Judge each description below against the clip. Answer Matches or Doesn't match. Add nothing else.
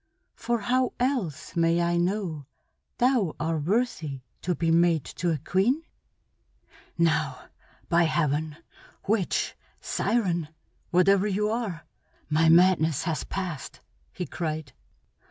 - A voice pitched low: Doesn't match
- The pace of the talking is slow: Matches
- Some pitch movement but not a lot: Matches